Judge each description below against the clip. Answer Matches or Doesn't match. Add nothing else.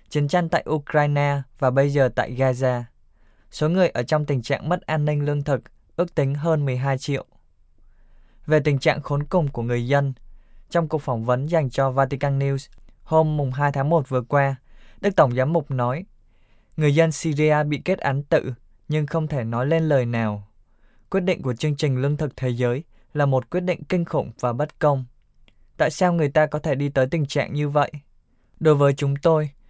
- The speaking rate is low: Doesn't match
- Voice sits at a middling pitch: Matches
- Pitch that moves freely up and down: Doesn't match